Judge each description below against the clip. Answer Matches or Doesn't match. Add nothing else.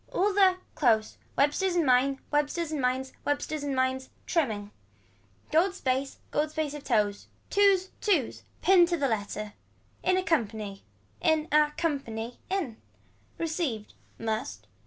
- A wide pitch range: Matches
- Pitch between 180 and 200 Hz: Doesn't match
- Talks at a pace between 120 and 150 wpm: Matches